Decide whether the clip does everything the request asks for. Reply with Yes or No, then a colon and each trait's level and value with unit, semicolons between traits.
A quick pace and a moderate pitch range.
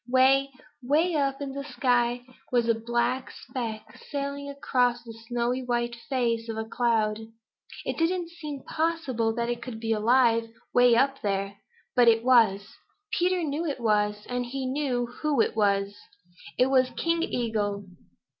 No: average, 160 wpm; average, 3.3 semitones